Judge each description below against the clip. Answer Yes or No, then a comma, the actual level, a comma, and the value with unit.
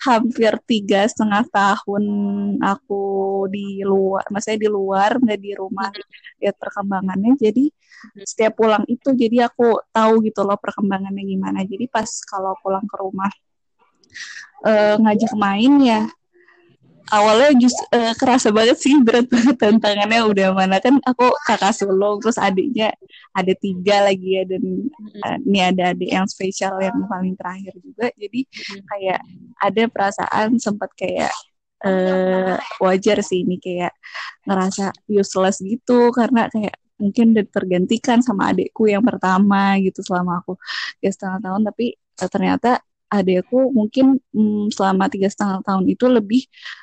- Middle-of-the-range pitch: No, high, 205 Hz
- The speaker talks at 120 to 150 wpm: Yes, fast, 140 wpm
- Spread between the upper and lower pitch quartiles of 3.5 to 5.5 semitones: No, average, 3.0 semitones